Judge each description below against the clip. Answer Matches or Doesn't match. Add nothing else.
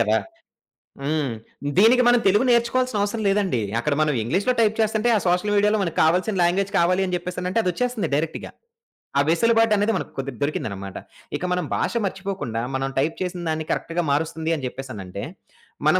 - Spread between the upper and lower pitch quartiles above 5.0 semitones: Matches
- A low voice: Doesn't match